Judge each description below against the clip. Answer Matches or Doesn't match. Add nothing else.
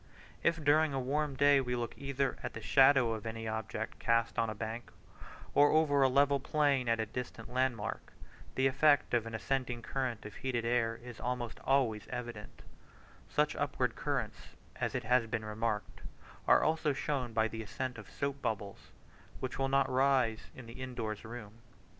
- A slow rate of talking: Doesn't match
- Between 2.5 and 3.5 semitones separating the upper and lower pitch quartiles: Matches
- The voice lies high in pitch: Doesn't match